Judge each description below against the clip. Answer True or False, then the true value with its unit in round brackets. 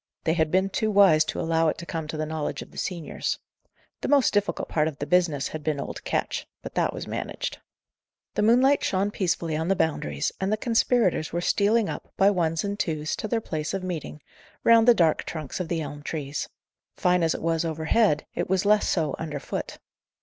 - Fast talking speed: True (215 wpm)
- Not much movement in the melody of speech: False (4.3 semitones)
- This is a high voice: False (170 Hz)